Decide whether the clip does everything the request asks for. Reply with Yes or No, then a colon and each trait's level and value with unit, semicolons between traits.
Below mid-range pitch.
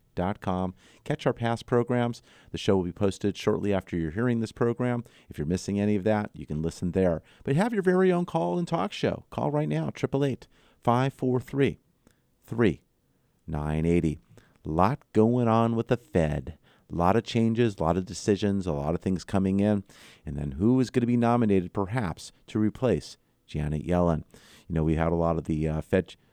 Yes: low, 100 Hz